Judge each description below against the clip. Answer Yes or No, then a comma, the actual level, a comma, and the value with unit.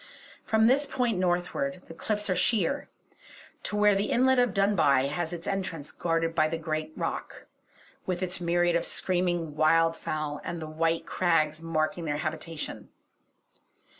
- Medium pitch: Yes, medium, 170 Hz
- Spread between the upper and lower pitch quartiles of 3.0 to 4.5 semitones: Yes, average, 3.5 semitones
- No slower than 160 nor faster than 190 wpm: No, average, 150 wpm